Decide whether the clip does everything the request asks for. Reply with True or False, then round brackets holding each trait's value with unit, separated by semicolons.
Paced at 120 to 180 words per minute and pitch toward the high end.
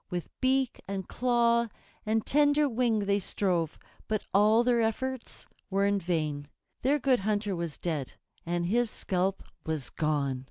True (150 wpm; 205 Hz)